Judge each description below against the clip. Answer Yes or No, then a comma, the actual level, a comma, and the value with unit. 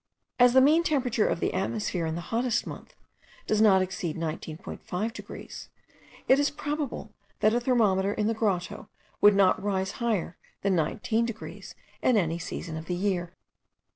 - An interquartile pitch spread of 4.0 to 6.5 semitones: Yes, average, 4.7 semitones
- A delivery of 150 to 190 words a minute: Yes, average, 165 wpm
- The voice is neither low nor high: No, high, 205 Hz